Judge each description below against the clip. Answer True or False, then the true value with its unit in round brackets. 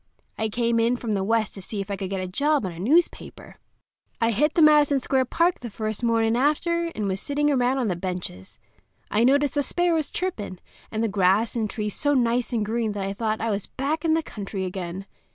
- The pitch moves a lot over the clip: True (6.1 semitones)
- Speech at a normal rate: False (225 wpm)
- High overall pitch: True (230 Hz)